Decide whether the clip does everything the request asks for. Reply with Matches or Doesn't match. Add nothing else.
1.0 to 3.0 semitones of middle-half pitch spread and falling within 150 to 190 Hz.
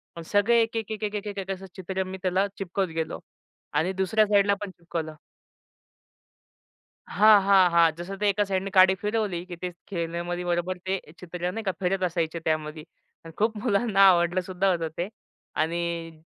Matches